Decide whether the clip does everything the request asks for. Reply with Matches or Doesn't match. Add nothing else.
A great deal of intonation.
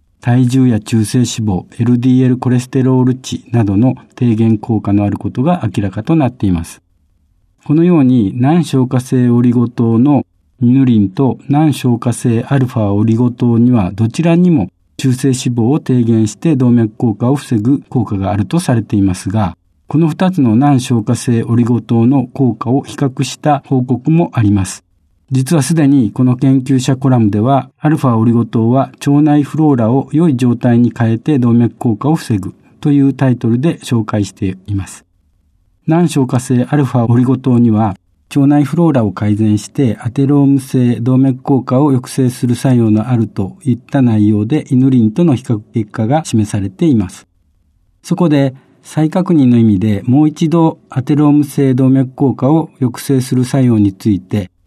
Doesn't match